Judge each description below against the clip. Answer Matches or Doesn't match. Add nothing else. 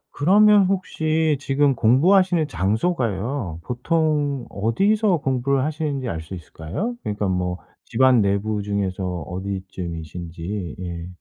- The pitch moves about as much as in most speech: Doesn't match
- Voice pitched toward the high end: Doesn't match